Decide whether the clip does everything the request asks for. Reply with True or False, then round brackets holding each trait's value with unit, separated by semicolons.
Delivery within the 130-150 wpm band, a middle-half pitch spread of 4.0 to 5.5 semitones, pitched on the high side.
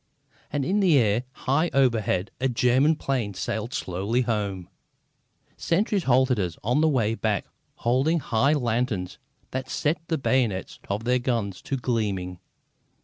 False (145 wpm; 4.5 semitones; 125 Hz)